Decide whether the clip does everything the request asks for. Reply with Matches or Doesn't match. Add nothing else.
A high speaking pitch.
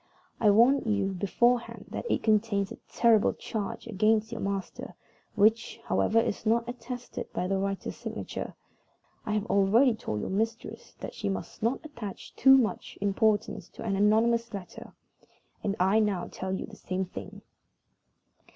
Matches